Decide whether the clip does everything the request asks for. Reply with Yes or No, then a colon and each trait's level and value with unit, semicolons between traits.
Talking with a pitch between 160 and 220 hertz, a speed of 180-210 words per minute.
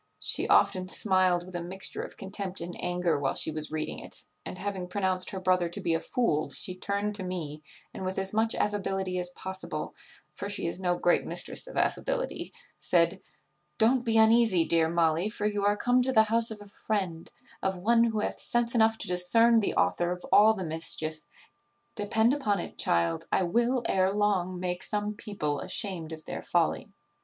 Yes: high, 190 Hz; average, 195 wpm